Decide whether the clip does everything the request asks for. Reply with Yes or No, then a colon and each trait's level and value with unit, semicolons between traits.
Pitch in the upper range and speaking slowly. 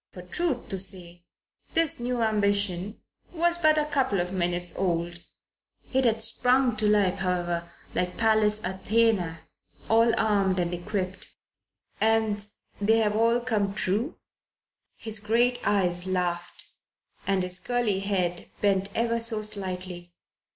Yes: high, 205 Hz; slow, 130 wpm